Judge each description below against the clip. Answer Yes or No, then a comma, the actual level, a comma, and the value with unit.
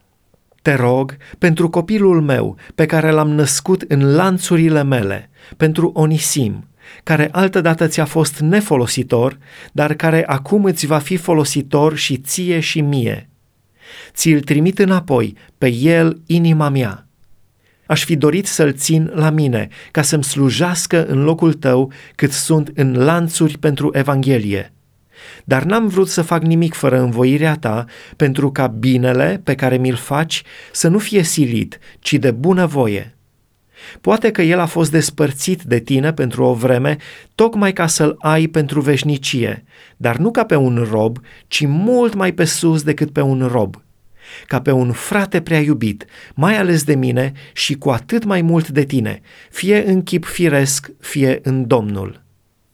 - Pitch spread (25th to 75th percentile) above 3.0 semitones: Yes, average, 4.4 semitones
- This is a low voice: No, medium, 150 Hz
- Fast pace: No, average, 155 wpm